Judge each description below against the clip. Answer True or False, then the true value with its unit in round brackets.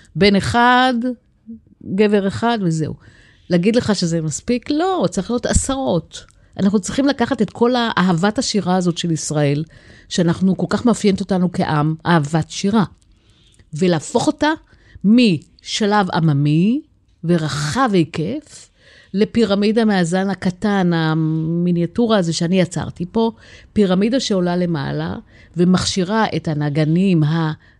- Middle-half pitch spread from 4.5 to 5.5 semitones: True (5.2 semitones)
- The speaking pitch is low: False (185 Hz)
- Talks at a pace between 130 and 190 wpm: False (110 wpm)